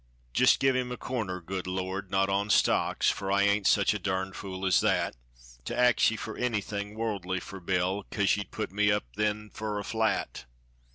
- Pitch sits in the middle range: No, low, 100 Hz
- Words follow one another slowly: No, average, 195 wpm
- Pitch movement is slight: Yes, narrow, 2.2 semitones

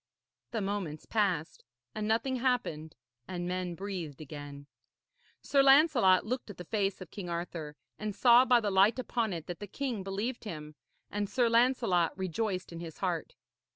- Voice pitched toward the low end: No, high, 195 Hz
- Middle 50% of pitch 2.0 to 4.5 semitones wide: No, average, 5.2 semitones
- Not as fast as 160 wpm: No, average, 165 wpm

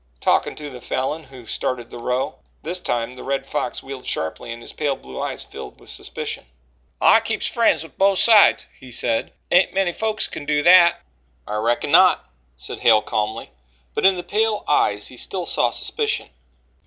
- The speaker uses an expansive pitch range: Yes, wide, 7.3 semitones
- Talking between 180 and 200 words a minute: Yes, average, 185 wpm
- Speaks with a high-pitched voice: No, medium, 140 Hz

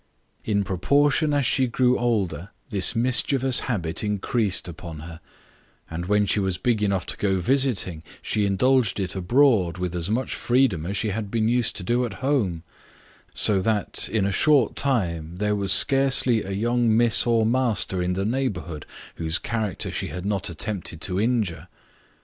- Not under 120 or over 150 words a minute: No, average, 175 wpm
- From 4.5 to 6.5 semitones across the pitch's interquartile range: Yes, average, 4.9 semitones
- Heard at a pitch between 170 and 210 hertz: No, low, 105 Hz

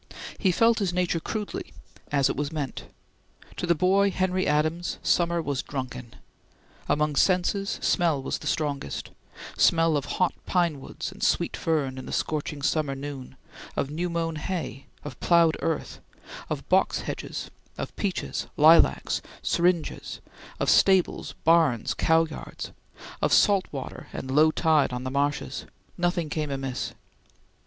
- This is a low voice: No, medium, 160 Hz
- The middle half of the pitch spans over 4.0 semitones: No, average, 3.6 semitones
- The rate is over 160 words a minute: No, average, 145 wpm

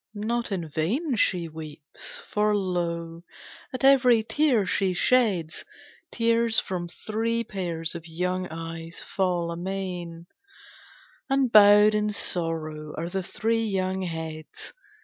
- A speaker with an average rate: No, slow, 120 wpm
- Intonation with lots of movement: No, average, 4.7 semitones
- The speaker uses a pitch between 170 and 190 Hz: Yes, medium, 185 Hz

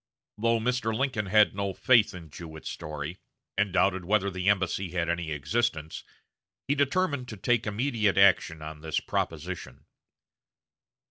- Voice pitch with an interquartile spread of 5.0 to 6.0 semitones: Yes, wide, 5.4 semitones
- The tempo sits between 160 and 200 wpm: No, average, 140 wpm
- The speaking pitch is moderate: No, low, 100 Hz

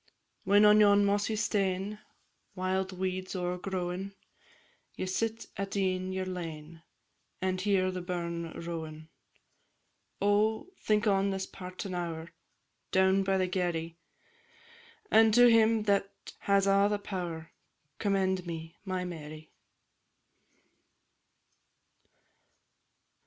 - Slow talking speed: Yes, slow, 105 wpm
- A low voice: No, high, 190 Hz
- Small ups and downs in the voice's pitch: Yes, narrow, 2.2 semitones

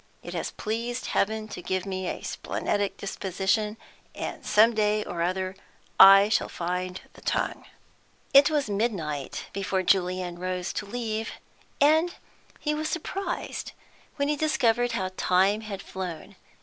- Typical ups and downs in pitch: Yes, average, 4.0 semitones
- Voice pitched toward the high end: Yes, high, 205 Hz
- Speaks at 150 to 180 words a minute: No, average, 140 wpm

